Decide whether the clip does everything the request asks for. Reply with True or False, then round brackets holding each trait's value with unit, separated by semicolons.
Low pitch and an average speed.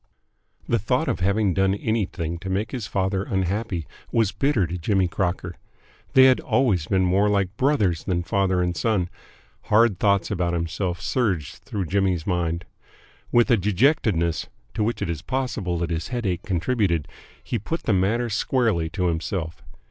True (95 Hz; 165 wpm)